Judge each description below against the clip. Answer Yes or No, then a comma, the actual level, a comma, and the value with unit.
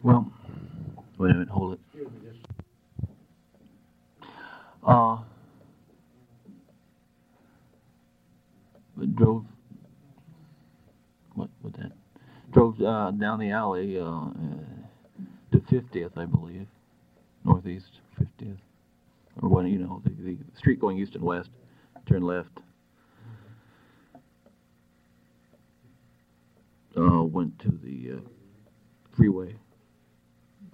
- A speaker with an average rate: No, slow, 85 wpm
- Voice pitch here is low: Yes, very low, 90 Hz